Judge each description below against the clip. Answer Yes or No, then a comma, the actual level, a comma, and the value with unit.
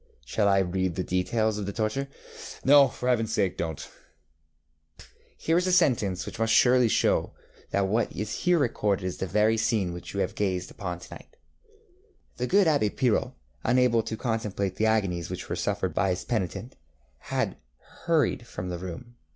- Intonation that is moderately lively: Yes, average, 4.7 semitones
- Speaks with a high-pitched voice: No, low, 110 Hz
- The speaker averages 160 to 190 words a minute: Yes, average, 185 wpm